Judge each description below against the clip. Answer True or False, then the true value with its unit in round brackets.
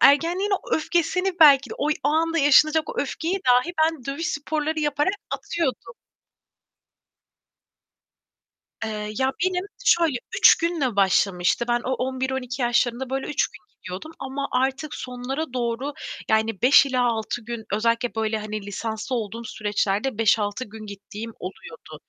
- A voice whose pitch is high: True (255 Hz)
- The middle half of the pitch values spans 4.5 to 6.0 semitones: True (5.6 semitones)